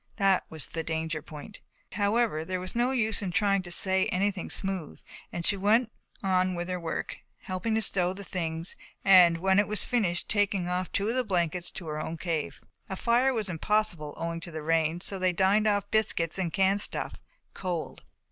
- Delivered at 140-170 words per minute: No, average, 195 wpm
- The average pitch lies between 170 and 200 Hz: Yes, medium, 185 Hz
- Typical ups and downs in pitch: Yes, average, 3.3 semitones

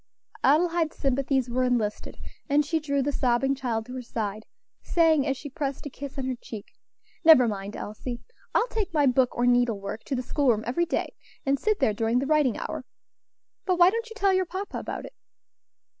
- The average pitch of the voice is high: Yes, very high, 270 Hz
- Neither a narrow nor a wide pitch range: Yes, average, 4.6 semitones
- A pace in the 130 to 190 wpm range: No, fast, 205 wpm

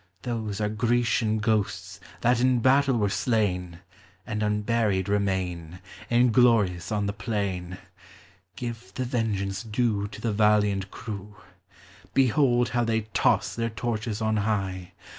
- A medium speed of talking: No, slow, 125 wpm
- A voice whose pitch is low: Yes, low, 110 Hz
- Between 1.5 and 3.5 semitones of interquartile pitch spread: Yes, average, 2.8 semitones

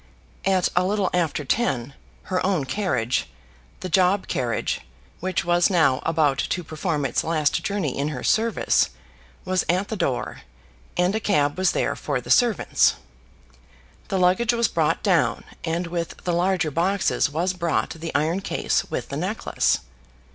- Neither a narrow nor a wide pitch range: Yes, average, 4.0 semitones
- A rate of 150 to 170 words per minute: Yes, average, 155 wpm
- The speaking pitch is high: No, medium, 175 Hz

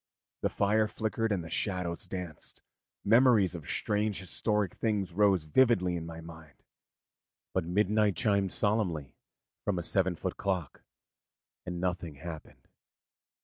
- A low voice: Yes, very low, 95 Hz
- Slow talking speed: Yes, slow, 130 wpm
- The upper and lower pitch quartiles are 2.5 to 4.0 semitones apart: Yes, average, 3.6 semitones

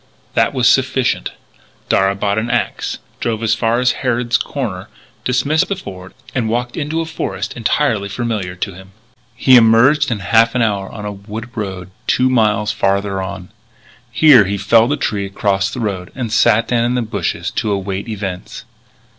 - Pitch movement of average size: Yes, average, 3.8 semitones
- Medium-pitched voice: No, low, 110 Hz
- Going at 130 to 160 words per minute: No, average, 175 wpm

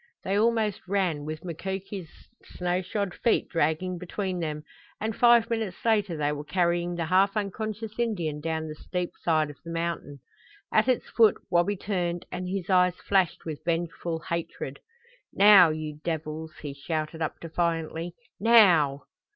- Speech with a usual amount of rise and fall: Yes, average, 3.8 semitones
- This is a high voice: No, medium, 175 Hz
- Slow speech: No, average, 150 wpm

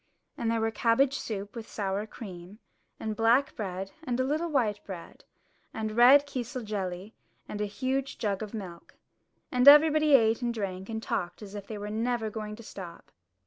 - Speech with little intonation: No, average, 3.5 semitones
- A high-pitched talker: Yes, high, 220 Hz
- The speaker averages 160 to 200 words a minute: Yes, average, 185 wpm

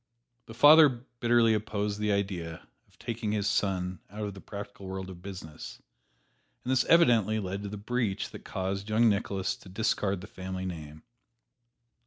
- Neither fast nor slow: Yes, average, 165 wpm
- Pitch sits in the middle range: No, low, 100 Hz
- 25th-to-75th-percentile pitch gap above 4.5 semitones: No, average, 3.0 semitones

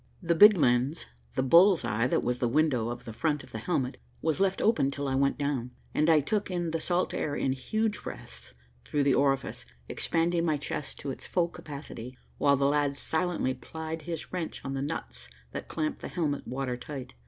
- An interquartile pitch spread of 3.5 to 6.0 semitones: Yes, average, 4.0 semitones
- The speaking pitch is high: No, medium, 145 Hz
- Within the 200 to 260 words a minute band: Yes, fast, 205 wpm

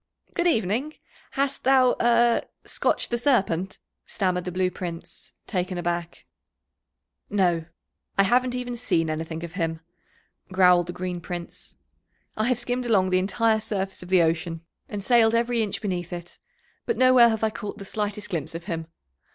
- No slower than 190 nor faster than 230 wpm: No, average, 160 wpm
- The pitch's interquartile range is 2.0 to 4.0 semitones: No, average, 5.2 semitones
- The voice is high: Yes, high, 195 Hz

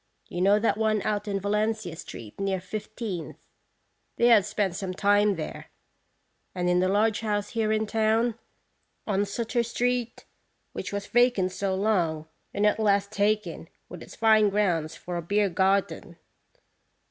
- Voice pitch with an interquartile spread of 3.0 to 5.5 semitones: No, narrow, 2.4 semitones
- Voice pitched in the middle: No, high, 205 Hz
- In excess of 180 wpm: No, average, 155 wpm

